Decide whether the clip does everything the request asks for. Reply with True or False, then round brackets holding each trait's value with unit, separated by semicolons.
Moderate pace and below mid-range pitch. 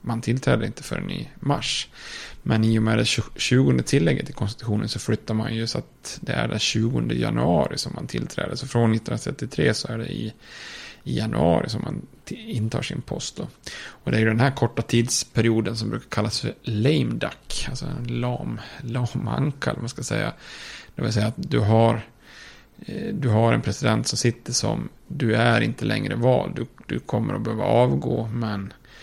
True (185 wpm; 115 Hz)